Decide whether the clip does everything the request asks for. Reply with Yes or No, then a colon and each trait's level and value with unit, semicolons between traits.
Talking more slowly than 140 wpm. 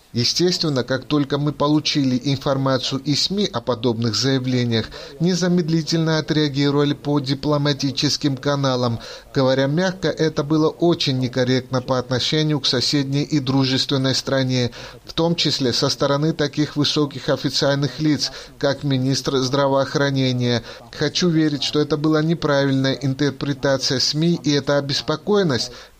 Yes: average, 120 wpm